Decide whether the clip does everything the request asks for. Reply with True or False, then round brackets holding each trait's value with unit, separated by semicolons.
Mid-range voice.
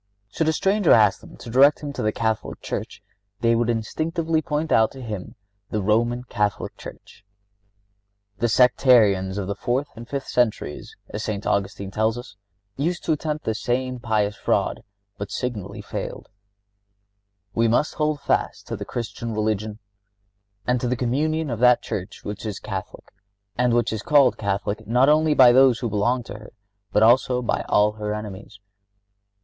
False (120 Hz)